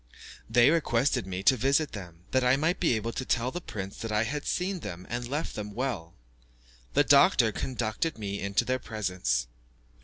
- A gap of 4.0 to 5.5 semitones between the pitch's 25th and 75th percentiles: Yes, average, 5.2 semitones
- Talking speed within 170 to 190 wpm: Yes, average, 185 wpm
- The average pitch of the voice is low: Yes, low, 115 Hz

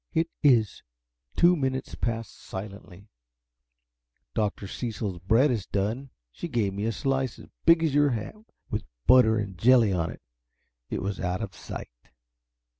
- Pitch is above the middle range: No, low, 110 Hz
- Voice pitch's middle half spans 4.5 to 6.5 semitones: Yes, average, 5.0 semitones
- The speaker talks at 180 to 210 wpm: No, average, 150 wpm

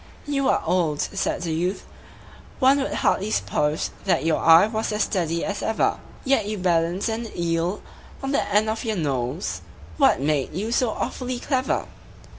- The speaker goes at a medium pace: Yes, average, 170 wpm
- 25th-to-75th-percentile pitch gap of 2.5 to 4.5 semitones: No, average, 5.3 semitones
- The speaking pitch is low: No, high, 190 Hz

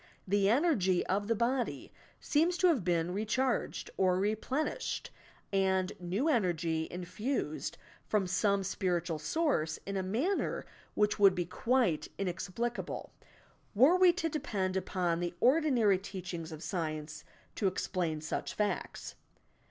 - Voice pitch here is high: Yes, high, 195 Hz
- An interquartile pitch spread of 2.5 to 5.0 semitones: No, wide, 5.4 semitones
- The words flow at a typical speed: No, slow, 130 wpm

